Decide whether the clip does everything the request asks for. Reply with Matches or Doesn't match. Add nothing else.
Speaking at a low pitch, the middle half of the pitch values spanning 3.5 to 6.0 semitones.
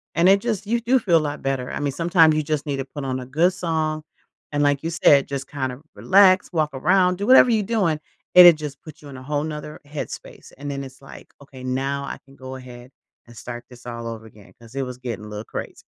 Doesn't match